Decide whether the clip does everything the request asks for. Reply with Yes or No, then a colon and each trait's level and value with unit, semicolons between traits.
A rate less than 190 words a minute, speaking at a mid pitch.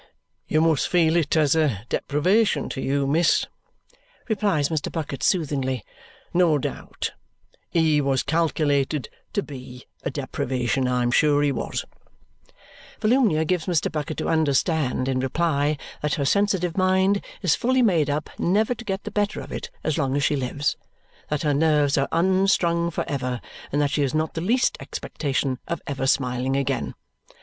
Yes: average, 160 wpm; medium, 150 Hz